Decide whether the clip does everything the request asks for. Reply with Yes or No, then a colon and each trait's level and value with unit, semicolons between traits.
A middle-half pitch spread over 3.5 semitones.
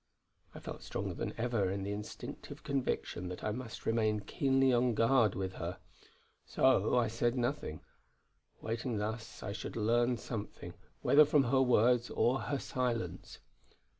No: average, 3.2 semitones